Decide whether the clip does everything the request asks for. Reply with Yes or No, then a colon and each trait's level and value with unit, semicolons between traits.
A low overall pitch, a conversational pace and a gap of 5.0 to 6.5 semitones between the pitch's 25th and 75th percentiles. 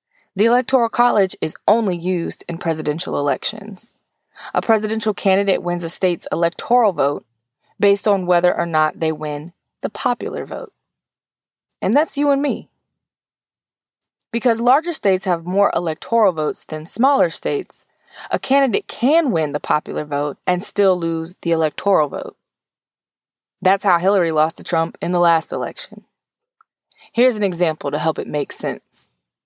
No: medium, 185 Hz; average, 150 wpm; wide, 5.6 semitones